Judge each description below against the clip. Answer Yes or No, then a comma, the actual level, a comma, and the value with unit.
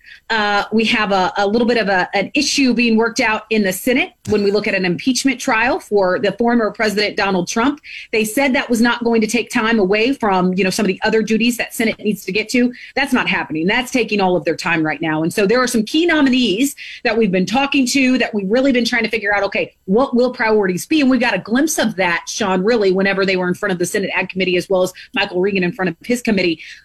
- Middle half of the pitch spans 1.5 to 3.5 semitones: No, average, 4.2 semitones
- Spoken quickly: Yes, fast, 265 wpm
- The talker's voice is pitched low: No, high, 220 Hz